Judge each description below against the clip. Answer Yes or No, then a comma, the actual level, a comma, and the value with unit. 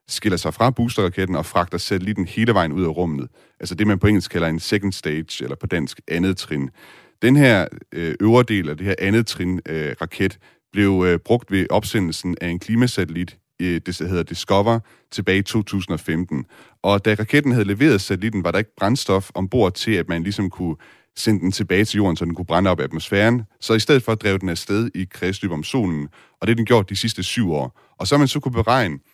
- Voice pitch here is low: Yes, very low, 95 Hz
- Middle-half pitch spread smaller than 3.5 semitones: No, average, 4.1 semitones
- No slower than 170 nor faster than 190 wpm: No, average, 210 wpm